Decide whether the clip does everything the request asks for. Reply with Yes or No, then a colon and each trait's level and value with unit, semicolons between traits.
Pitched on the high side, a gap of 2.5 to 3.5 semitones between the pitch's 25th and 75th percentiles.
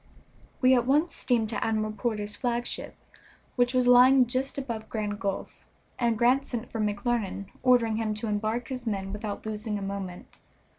Yes: high, 225 Hz; average, 2.8 semitones